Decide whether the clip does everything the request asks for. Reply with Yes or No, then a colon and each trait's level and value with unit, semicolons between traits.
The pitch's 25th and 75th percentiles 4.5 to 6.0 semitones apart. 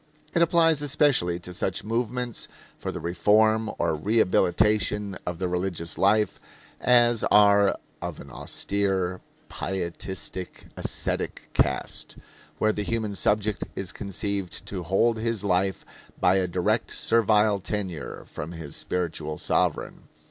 No: average, 3.3 semitones